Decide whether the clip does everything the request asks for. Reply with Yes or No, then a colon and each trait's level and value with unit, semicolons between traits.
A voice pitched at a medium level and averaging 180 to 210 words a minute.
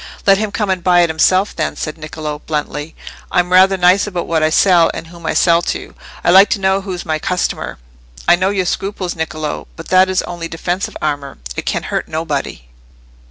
Yes: medium, 175 Hz; fast, 205 wpm